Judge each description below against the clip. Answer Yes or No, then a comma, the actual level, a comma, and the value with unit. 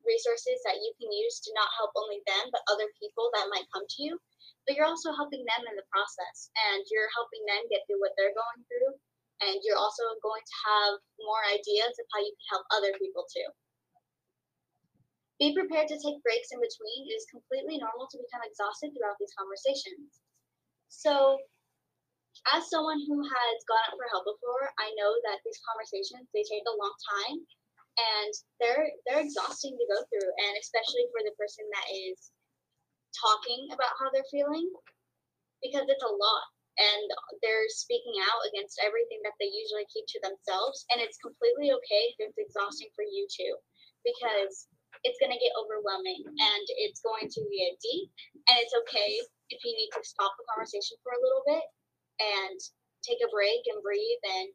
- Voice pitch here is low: No, high, 245 Hz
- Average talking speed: Yes, average, 185 wpm